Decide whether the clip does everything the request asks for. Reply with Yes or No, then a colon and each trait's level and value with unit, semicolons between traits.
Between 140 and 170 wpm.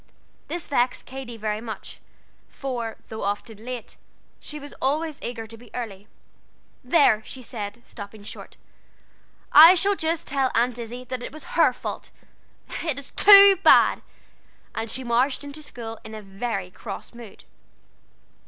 Yes: average, 150 wpm